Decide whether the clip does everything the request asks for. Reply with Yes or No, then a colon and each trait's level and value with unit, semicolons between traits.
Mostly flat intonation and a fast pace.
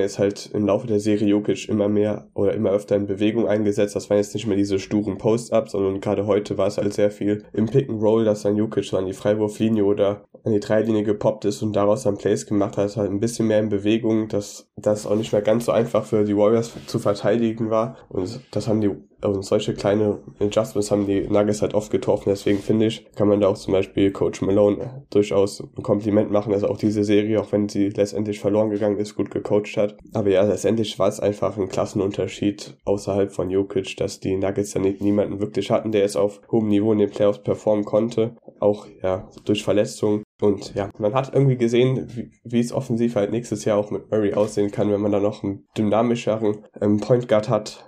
Yes: narrow, 1.2 semitones; fast, 220 wpm